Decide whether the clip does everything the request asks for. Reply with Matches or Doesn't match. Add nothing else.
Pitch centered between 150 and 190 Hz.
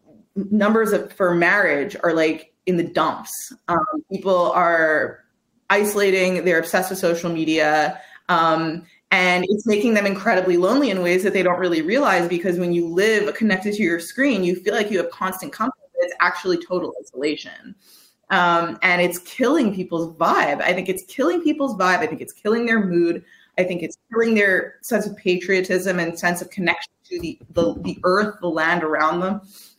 Matches